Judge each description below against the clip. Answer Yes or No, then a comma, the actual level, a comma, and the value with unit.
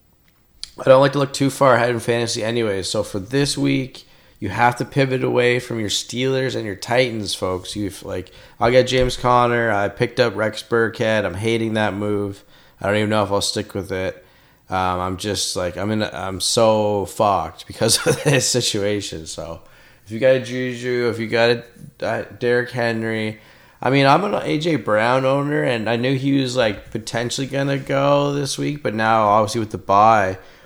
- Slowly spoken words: No, average, 200 wpm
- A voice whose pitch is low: Yes, low, 115 Hz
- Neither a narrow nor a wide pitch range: Yes, average, 3.7 semitones